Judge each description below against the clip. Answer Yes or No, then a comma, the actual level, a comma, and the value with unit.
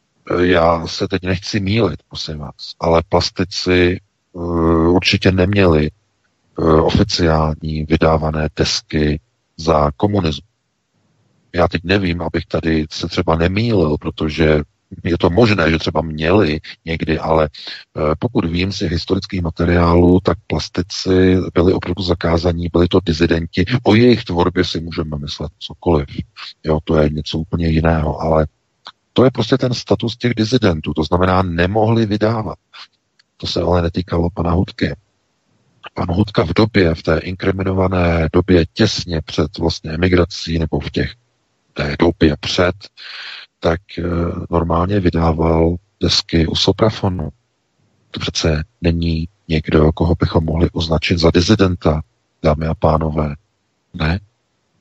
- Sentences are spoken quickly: No, average, 125 wpm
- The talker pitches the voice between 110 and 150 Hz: No, very low, 85 Hz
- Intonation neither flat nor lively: Yes, average, 3.0 semitones